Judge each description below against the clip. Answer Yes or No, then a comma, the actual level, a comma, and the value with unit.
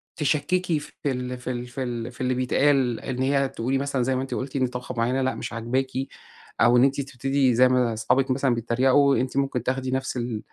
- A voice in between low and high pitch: No, low, 130 Hz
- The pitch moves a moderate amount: No, narrow, 1.7 semitones